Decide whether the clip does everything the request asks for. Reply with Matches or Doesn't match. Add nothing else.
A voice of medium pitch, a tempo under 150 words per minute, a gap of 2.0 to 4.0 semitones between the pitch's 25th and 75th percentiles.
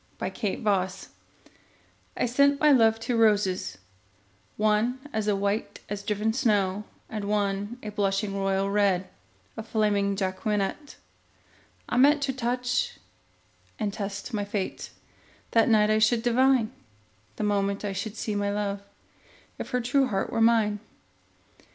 Doesn't match